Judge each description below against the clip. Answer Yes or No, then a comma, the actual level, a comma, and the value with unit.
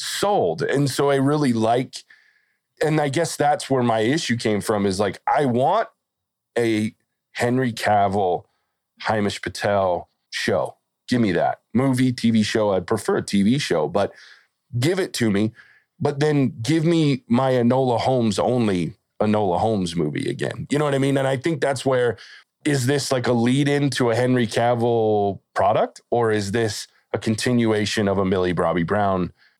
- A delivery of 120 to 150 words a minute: No, average, 170 wpm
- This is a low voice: Yes, low, 120 Hz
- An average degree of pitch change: Yes, average, 4.5 semitones